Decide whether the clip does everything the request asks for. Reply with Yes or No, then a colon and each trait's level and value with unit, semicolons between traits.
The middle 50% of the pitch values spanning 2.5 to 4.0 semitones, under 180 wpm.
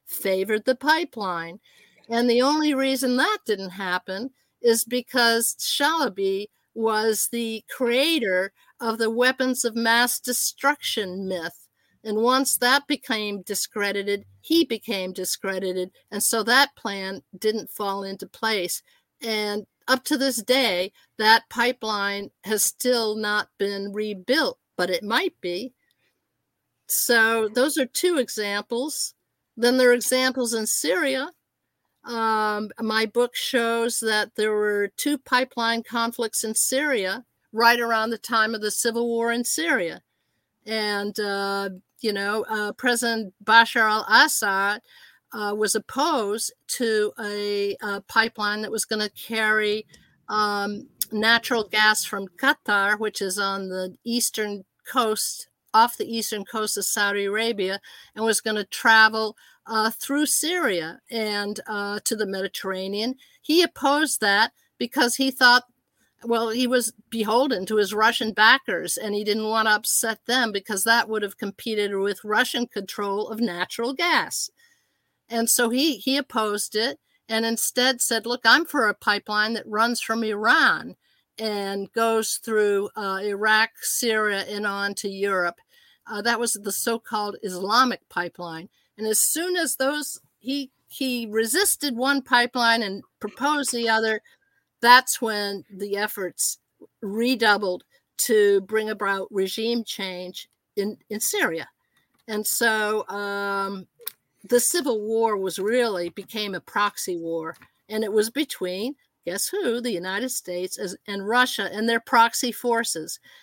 Yes: average, 3.1 semitones; average, 140 wpm